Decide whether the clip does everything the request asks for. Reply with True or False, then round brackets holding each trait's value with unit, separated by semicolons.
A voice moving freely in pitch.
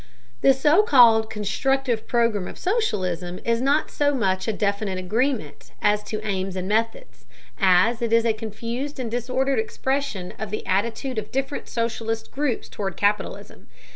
False (4.4 semitones)